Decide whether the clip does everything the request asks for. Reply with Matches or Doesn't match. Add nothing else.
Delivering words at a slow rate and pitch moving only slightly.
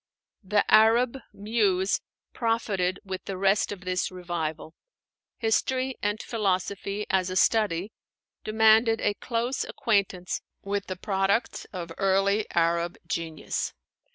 Doesn't match